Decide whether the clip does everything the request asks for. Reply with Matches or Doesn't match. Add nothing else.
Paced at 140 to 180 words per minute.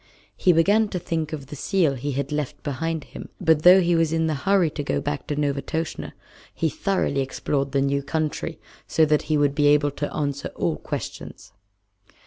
Doesn't match